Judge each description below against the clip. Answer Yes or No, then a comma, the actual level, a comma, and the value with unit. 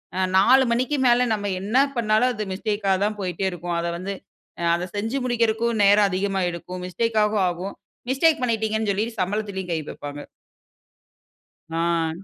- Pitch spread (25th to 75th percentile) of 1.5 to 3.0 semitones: No, average, 3.7 semitones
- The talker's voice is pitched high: Yes, high, 205 Hz